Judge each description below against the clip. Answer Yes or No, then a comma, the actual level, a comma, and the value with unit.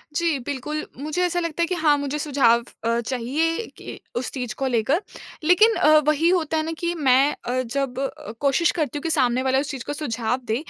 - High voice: Yes, very high, 285 Hz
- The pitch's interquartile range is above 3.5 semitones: Yes, average, 4.3 semitones